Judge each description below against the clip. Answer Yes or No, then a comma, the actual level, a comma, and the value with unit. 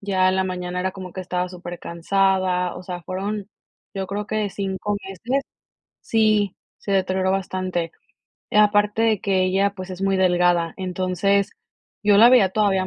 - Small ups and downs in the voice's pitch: Yes, narrow, 1.7 semitones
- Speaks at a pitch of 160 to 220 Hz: Yes, high, 190 Hz